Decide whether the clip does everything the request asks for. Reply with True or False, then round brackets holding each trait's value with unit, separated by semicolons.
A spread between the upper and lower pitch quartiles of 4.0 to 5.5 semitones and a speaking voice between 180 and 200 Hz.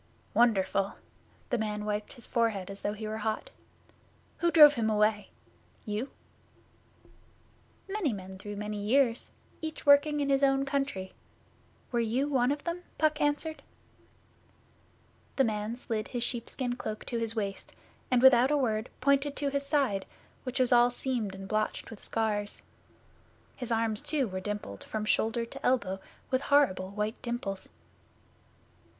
False (4.6 semitones; 235 Hz)